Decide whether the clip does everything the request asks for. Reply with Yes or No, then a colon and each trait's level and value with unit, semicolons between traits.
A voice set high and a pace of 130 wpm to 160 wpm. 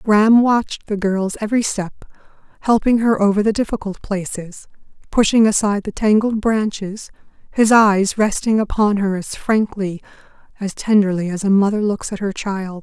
Yes: high, 205 Hz; average, 155 wpm